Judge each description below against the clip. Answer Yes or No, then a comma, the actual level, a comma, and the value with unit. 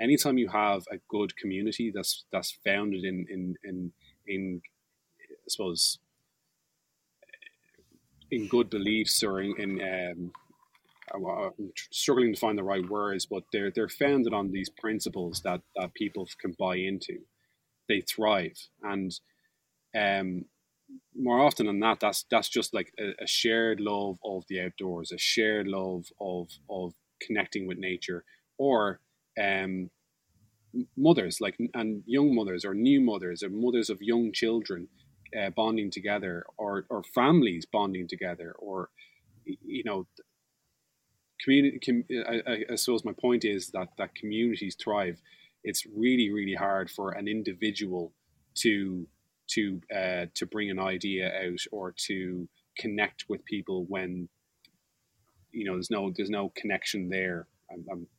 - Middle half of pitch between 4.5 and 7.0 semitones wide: No, average, 3.7 semitones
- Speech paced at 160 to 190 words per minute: No, average, 140 wpm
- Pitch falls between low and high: No, low, 100 Hz